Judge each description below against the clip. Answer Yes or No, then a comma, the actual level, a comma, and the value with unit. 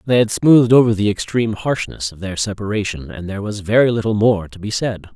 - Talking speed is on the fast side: Yes, fast, 220 wpm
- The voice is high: No, low, 105 Hz